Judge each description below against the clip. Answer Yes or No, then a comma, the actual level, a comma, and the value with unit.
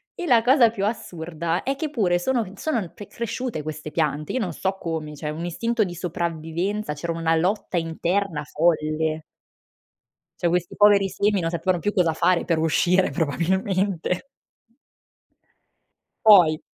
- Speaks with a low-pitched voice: No, medium, 175 Hz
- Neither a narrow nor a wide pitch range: Yes, average, 4.1 semitones